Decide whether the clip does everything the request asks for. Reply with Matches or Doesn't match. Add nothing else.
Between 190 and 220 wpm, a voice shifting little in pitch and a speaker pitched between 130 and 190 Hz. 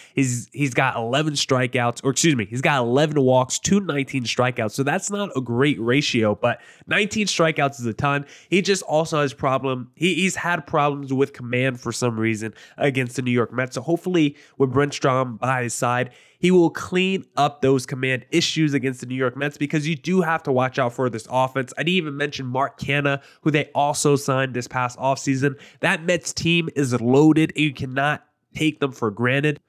Doesn't match